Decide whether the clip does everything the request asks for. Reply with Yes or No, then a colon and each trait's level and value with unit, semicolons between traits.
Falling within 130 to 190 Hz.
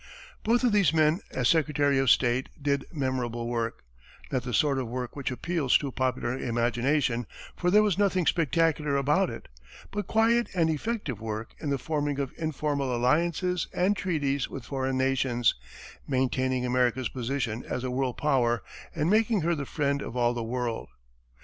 Yes: low, 135 Hz